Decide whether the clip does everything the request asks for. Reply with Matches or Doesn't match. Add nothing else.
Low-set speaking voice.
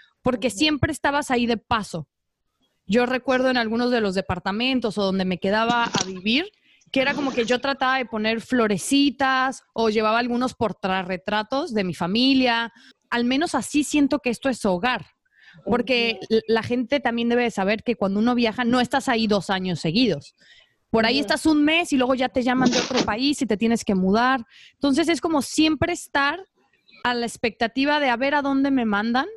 Doesn't match